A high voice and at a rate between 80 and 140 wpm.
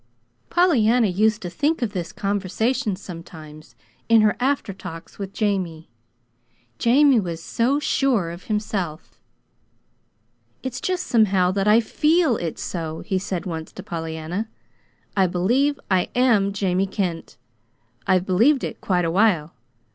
Yes: high, 195 Hz; slow, 135 wpm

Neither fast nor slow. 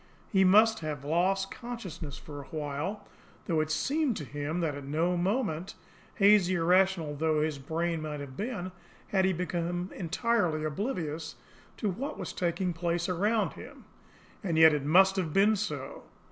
Yes: average, 165 wpm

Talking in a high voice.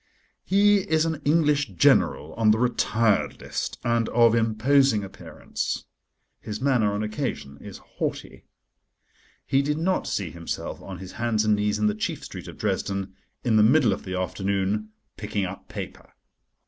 No: low, 110 Hz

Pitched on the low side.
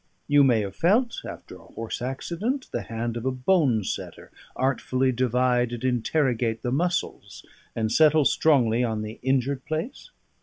Yes: low, 130 Hz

